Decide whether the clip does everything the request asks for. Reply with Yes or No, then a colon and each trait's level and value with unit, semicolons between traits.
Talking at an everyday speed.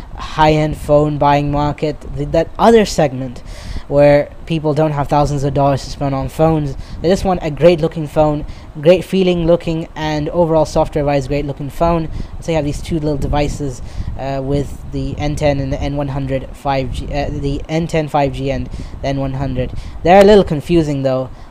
Yes: average, 180 wpm